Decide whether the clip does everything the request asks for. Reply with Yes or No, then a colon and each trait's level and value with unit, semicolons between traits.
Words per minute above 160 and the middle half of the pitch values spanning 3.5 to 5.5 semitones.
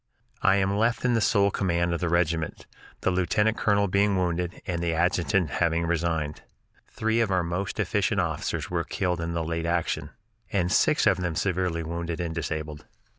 No: average, 175 wpm; average, 2.7 semitones